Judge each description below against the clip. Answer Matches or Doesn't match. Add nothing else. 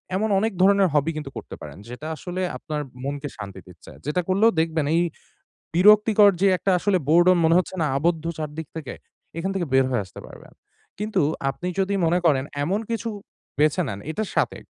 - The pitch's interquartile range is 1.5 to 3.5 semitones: Doesn't match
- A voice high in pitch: Doesn't match